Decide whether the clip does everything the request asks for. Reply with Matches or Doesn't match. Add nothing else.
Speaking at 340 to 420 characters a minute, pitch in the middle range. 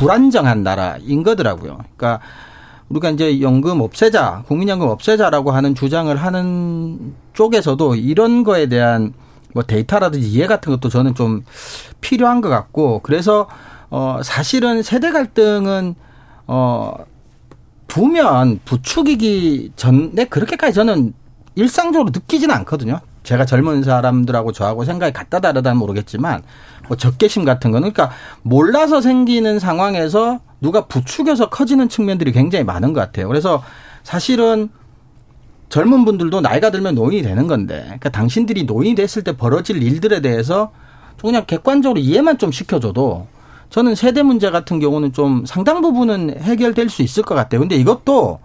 Matches